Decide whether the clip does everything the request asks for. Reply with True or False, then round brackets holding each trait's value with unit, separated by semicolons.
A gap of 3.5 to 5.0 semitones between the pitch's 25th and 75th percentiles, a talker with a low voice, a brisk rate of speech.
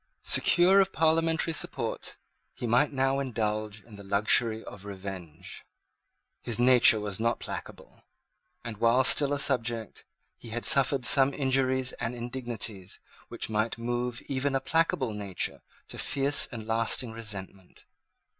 False (3.8 semitones; 120 Hz; 135 wpm)